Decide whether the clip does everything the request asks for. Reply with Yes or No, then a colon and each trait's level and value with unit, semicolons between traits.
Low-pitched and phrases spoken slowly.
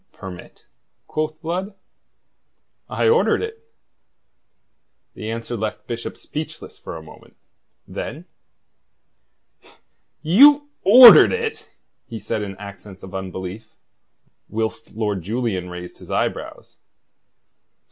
Yes: low, 115 Hz; slow, 100 wpm